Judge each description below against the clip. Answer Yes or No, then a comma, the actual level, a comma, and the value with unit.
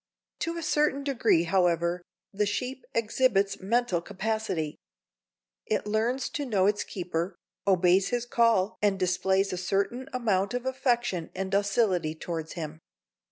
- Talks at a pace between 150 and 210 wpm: No, slow, 135 wpm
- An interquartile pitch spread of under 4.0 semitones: No, average, 4.9 semitones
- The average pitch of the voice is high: Yes, high, 200 Hz